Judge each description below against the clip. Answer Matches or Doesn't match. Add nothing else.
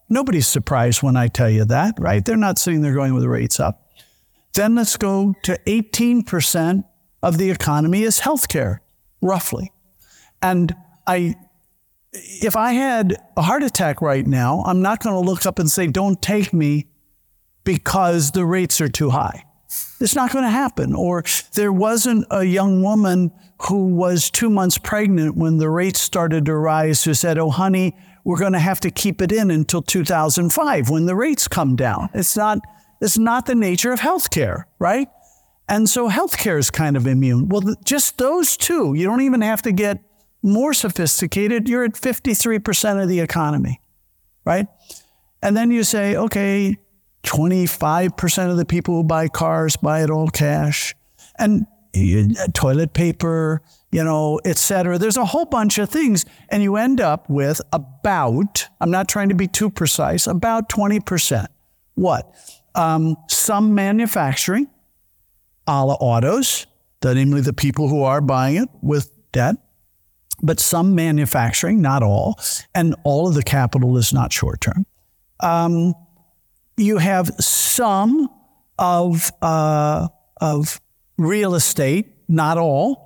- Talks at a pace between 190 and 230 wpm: Doesn't match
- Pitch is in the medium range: Matches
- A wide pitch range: Matches